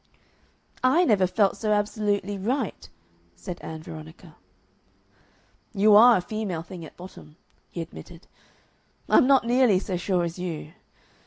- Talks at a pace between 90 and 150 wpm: Yes, slow, 135 wpm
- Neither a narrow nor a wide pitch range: Yes, average, 4.0 semitones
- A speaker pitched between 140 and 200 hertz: Yes, high, 190 Hz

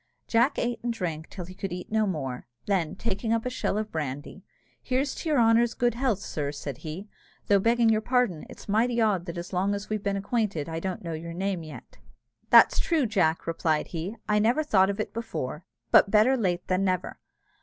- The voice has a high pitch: Yes, high, 200 Hz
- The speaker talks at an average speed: No, fast, 210 wpm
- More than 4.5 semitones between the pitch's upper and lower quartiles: Yes, average, 5.1 semitones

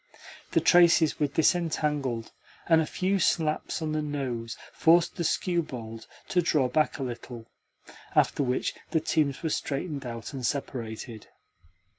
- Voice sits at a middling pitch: Yes, medium, 145 Hz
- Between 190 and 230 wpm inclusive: No, average, 140 wpm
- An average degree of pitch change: Yes, average, 4.6 semitones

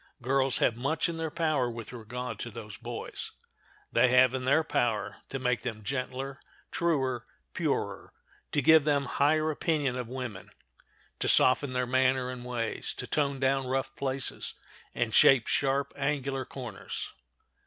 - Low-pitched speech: Yes, low, 130 Hz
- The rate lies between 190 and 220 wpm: No, average, 155 wpm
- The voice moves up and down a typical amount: No, narrow, 2.2 semitones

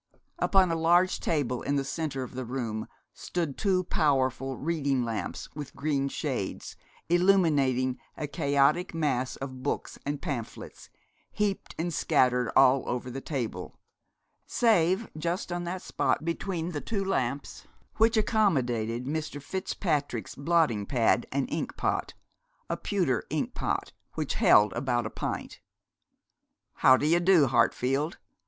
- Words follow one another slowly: Yes, slow, 130 wpm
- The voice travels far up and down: No, average, 5.0 semitones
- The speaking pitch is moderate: Yes, medium, 145 Hz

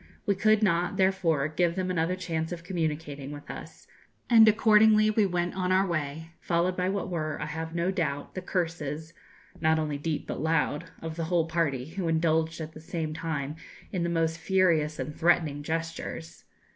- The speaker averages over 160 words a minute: Yes, average, 185 wpm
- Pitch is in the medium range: Yes, medium, 165 Hz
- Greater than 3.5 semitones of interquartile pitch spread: No, average, 2.7 semitones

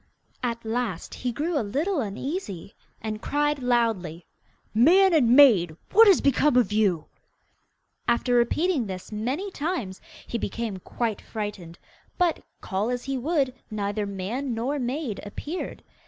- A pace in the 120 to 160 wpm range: Yes, average, 140 wpm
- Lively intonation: Yes, wide, 5.8 semitones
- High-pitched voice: Yes, high, 240 Hz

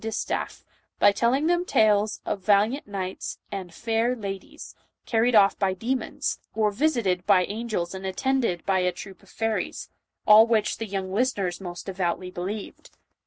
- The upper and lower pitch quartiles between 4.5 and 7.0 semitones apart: No, average, 3.3 semitones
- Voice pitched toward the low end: No, high, 205 Hz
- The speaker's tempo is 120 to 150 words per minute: No, average, 165 wpm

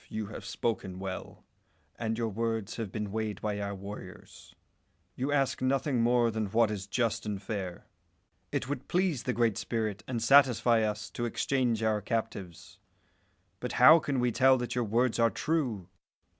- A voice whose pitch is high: No, low, 115 Hz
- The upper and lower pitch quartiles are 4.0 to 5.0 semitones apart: No, average, 3.0 semitones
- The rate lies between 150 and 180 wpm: Yes, average, 170 wpm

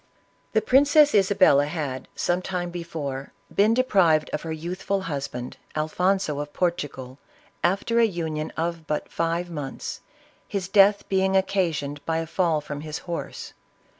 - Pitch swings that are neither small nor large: Yes, average, 4.0 semitones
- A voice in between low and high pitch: Yes, medium, 170 Hz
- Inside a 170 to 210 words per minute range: No, average, 145 wpm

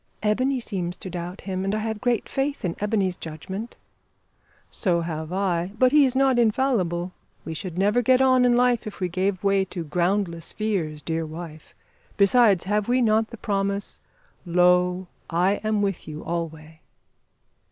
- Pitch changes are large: No, average, 4.3 semitones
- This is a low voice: No, high, 195 Hz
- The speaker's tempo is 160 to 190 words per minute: Yes, average, 165 wpm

